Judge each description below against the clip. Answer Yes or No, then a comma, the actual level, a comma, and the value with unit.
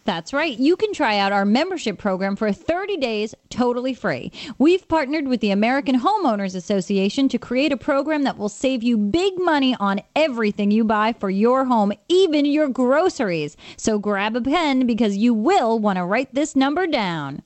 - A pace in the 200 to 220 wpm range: No, average, 185 wpm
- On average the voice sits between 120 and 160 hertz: No, high, 245 Hz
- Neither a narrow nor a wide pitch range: No, wide, 5.9 semitones